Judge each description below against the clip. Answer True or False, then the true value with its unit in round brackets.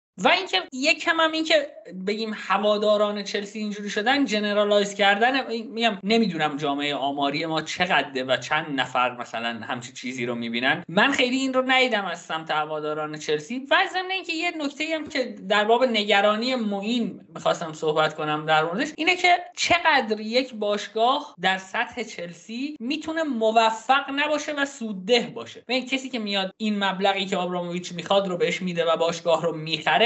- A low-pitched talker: False (210 Hz)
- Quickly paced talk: True (170 wpm)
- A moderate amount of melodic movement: False (7.5 semitones)